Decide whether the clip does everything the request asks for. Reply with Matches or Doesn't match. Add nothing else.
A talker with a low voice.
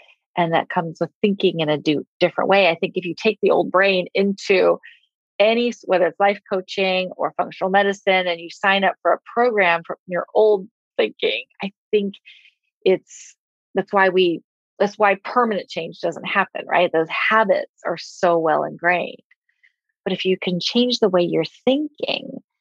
Doesn't match